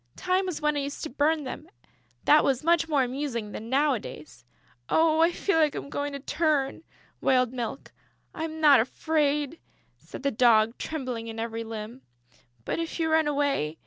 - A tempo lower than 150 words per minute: No, average, 175 wpm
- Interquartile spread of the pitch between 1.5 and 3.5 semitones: No, average, 4.6 semitones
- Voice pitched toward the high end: Yes, very high, 280 Hz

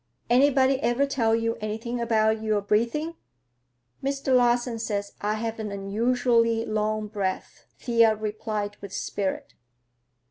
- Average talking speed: No, slow, 120 wpm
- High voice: Yes, high, 225 Hz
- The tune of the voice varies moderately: No, narrow, 2.3 semitones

